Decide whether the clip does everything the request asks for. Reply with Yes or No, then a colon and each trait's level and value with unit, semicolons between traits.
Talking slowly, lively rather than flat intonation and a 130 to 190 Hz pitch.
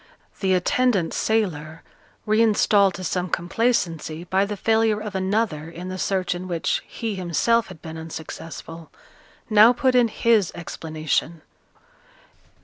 No: slow, 130 wpm; average, 4.7 semitones; medium, 185 Hz